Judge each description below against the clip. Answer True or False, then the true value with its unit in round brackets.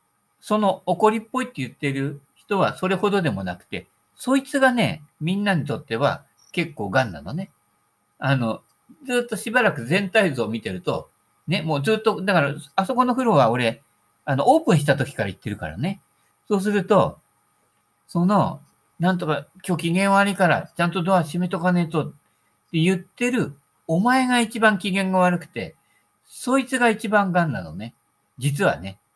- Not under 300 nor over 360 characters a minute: True (325 characters per minute)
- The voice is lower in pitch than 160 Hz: False (180 Hz)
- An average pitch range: False (6.7 semitones)